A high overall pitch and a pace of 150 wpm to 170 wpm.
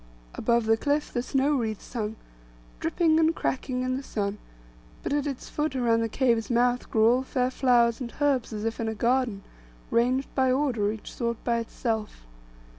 No: high, 245 Hz; average, 185 wpm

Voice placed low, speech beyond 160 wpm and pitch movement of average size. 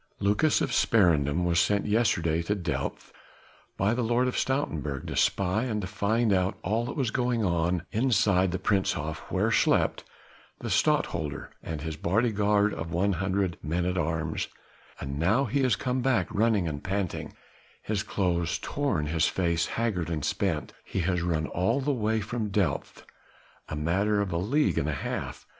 Yes: very low, 95 Hz; average, 170 wpm; average, 4.9 semitones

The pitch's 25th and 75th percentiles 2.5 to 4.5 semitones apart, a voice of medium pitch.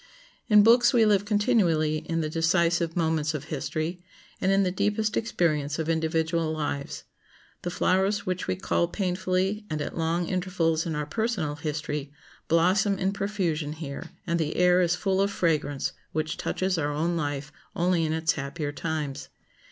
Yes: average, 3.5 semitones; medium, 170 Hz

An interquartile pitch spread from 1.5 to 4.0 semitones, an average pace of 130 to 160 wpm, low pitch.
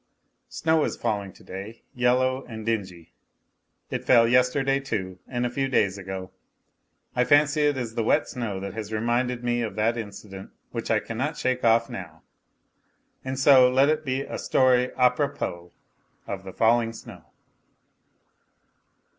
Yes: average, 3.6 semitones; average, 155 wpm; low, 120 Hz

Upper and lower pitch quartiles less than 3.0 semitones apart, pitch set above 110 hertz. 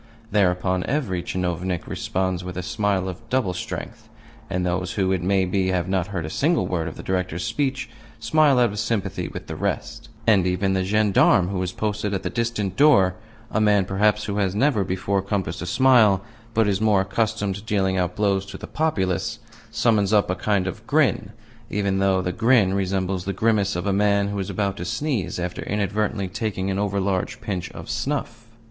No: narrow, 2.6 semitones; low, 100 Hz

